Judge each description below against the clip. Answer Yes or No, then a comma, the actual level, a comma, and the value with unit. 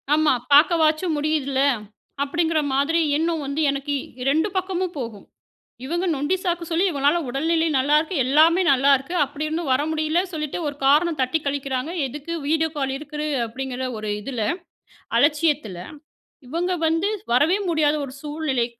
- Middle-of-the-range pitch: No, very high, 300 Hz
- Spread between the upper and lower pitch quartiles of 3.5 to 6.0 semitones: No, average, 3.0 semitones